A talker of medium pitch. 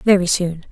Yes: medium, 180 Hz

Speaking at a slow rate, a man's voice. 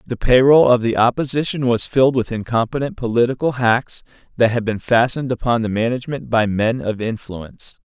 No: average, 175 wpm; male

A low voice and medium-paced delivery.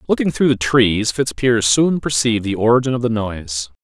Yes: low, 115 Hz; average, 190 wpm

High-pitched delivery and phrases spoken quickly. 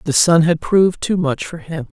No: medium, 165 Hz; fast, 240 wpm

